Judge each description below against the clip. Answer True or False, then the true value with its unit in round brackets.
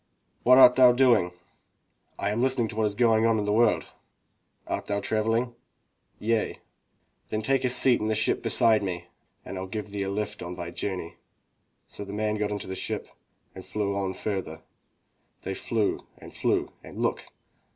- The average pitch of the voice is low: True (105 Hz)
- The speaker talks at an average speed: True (180 wpm)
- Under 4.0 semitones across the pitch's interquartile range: True (2.6 semitones)